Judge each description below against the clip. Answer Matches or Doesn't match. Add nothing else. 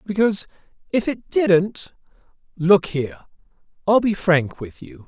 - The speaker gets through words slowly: Matches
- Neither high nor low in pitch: Matches